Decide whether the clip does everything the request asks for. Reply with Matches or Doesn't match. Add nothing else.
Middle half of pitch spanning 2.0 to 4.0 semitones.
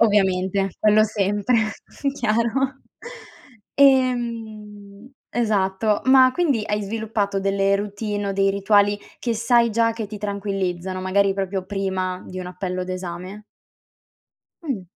Matches